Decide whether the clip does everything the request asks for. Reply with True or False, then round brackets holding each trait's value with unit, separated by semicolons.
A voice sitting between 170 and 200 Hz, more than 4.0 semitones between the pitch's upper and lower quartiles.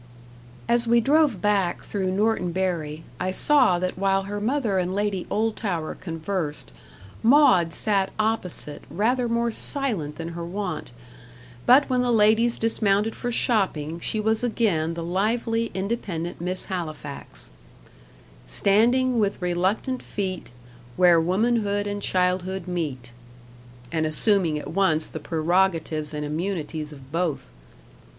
True (190 Hz; 4.9 semitones)